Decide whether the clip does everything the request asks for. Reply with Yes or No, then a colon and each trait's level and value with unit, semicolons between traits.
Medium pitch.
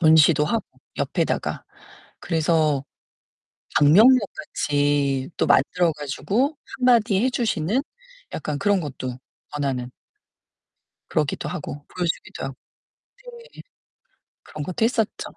Yes: medium, 160 Hz